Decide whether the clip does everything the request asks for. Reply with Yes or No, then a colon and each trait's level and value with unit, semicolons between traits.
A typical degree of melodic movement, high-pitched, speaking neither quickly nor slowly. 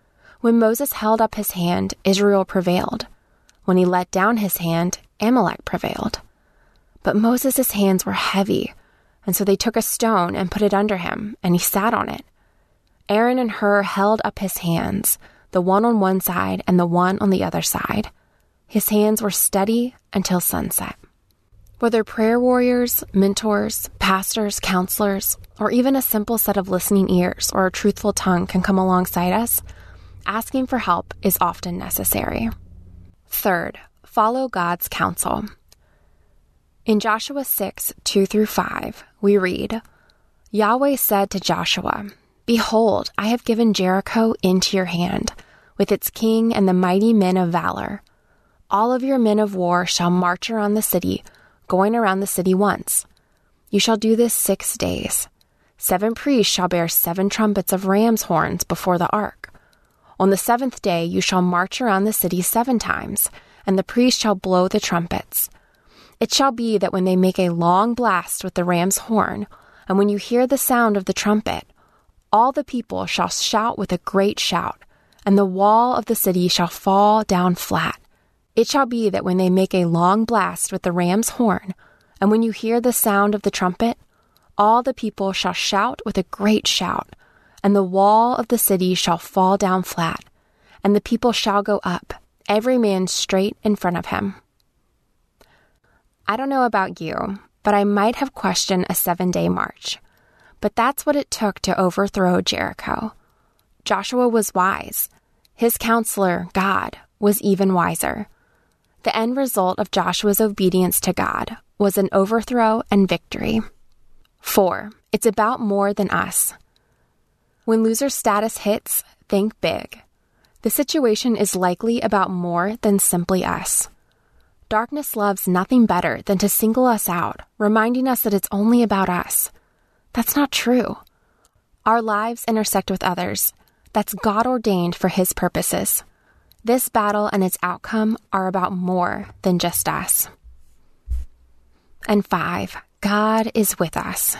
Yes: average, 3.4 semitones; high, 200 Hz; average, 160 wpm